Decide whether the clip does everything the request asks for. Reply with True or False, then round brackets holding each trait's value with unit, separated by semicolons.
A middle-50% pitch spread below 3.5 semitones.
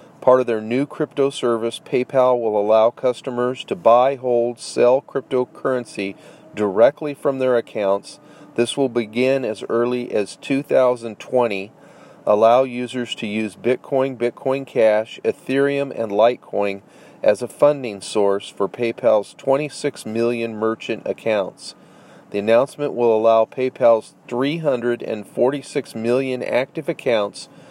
True (3.0 semitones)